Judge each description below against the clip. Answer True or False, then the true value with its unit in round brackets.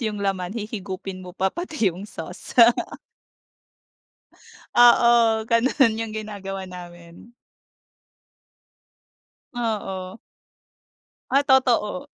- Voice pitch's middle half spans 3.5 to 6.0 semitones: True (3.9 semitones)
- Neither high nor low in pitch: False (210 Hz)